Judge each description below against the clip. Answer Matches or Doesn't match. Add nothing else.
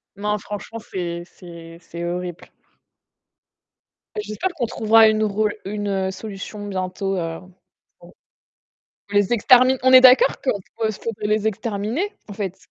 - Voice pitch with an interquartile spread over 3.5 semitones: Doesn't match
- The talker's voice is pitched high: Matches